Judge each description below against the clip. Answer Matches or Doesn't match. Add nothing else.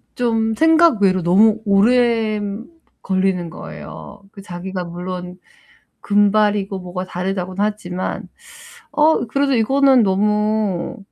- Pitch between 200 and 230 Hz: Matches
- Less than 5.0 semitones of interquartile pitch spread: Matches